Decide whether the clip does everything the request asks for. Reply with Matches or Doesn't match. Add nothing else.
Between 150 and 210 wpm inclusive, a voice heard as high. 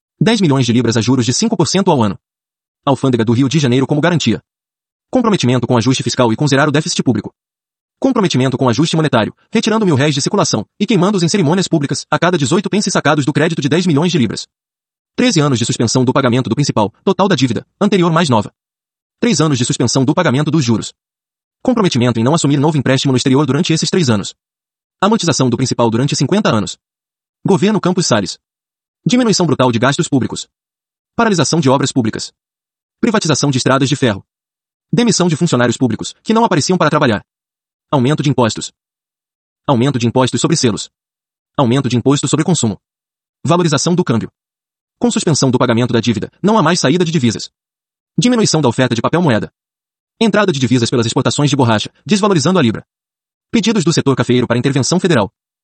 Doesn't match